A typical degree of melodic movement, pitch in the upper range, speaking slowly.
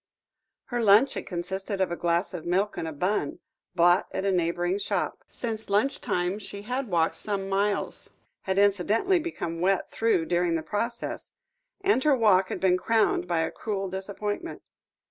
No: average, 3.4 semitones; high, 195 Hz; average, 170 wpm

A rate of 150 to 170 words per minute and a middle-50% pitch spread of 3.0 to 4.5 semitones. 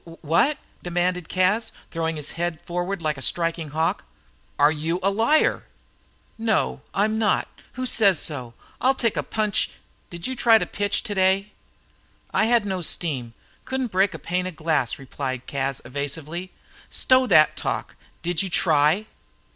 No: average, 160 wpm; average, 5.0 semitones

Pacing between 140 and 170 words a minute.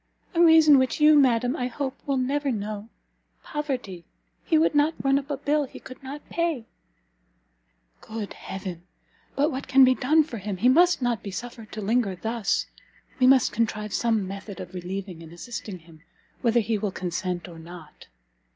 No: average, 180 wpm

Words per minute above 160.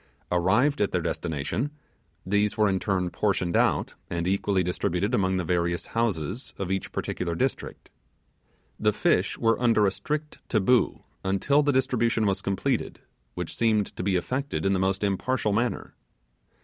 No: average, 155 wpm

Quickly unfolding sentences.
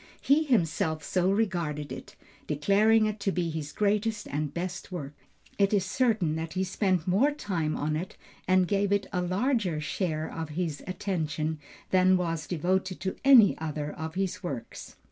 No: average, 165 wpm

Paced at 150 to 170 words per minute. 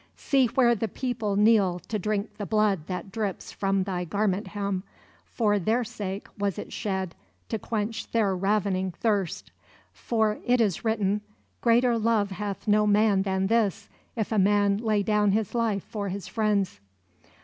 Yes: average, 160 wpm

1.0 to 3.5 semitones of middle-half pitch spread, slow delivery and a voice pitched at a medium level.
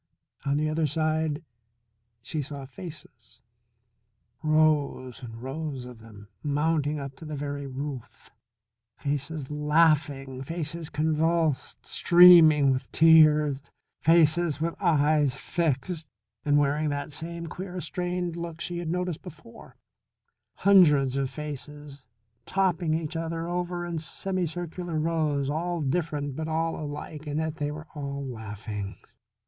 Yes: narrow, 2.6 semitones; slow, 120 wpm; medium, 150 Hz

